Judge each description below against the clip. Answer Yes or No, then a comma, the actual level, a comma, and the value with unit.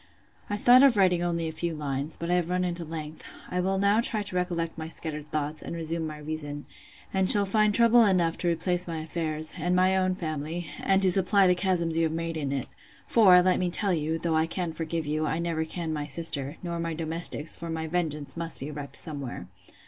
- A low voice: No, medium, 165 Hz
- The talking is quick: Yes, fast, 225 wpm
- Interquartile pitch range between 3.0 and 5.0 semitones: No, narrow, 2.6 semitones